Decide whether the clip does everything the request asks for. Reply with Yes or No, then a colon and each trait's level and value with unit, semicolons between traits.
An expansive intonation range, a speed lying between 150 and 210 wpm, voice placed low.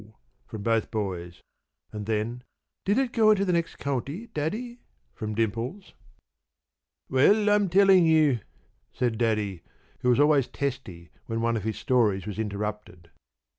No: wide, 8.1 semitones; average, 140 wpm; low, 120 Hz